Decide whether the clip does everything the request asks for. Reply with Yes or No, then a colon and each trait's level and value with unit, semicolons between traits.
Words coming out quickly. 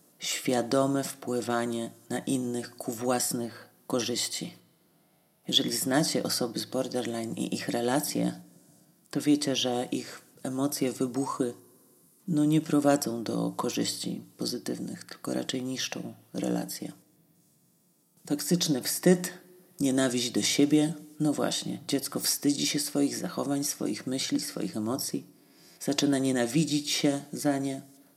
No: slow, 110 wpm